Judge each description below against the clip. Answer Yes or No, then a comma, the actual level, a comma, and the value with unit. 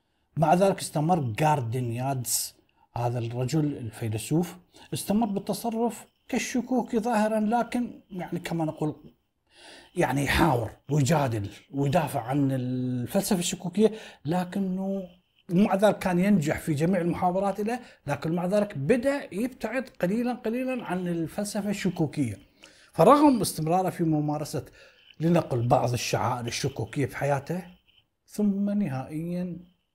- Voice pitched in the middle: Yes, medium, 170 Hz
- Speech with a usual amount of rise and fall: No, wide, 6.6 semitones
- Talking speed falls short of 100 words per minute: No, average, 105 wpm